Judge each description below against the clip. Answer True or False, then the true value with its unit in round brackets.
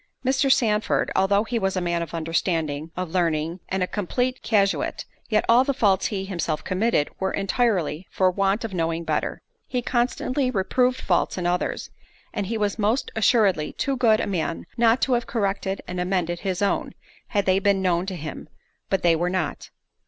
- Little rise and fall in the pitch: False (4.3 semitones)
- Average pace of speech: True (180 wpm)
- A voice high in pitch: True (195 Hz)